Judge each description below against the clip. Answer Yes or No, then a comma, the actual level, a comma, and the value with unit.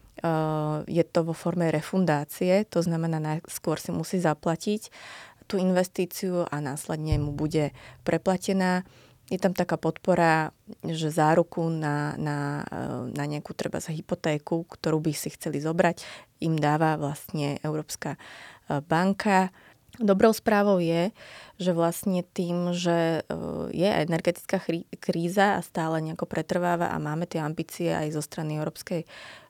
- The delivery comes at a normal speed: Yes, average, 130 wpm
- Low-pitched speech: No, medium, 165 Hz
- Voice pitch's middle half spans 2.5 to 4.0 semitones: Yes, average, 2.8 semitones